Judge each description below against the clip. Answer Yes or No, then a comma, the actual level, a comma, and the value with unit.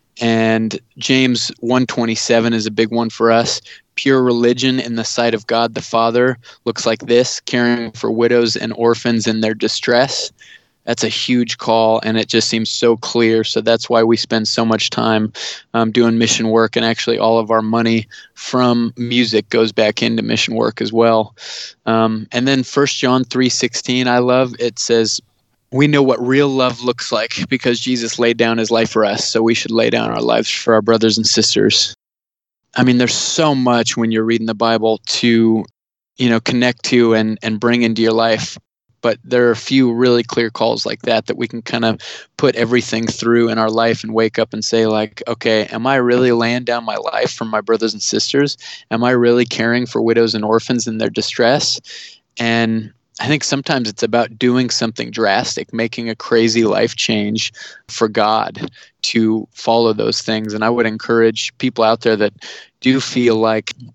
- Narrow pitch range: Yes, narrow, 1.4 semitones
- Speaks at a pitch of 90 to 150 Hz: Yes, low, 115 Hz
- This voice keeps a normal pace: Yes, average, 195 wpm